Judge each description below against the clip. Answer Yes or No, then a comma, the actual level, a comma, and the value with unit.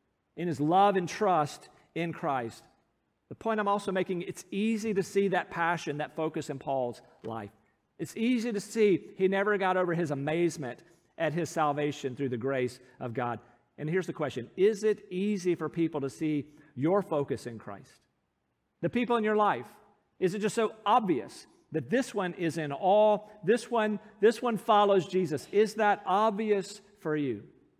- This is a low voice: No, medium, 180 Hz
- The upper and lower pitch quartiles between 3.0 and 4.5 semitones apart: No, wide, 5.6 semitones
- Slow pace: No, average, 180 wpm